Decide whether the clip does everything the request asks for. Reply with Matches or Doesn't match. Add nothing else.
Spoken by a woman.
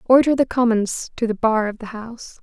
Matches